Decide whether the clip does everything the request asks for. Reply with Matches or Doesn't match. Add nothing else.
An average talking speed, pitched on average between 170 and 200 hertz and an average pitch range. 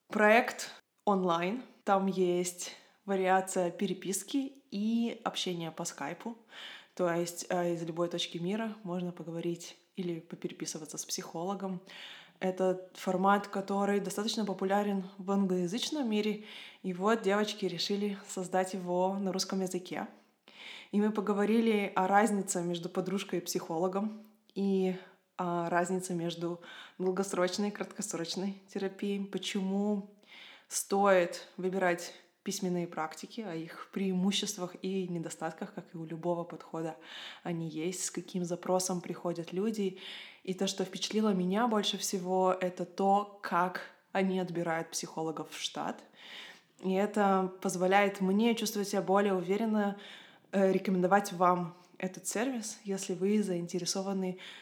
Doesn't match